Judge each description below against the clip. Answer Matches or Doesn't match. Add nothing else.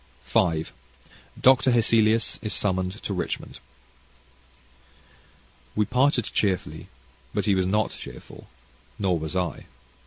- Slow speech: Matches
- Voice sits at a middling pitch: Doesn't match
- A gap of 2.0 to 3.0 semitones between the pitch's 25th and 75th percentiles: Doesn't match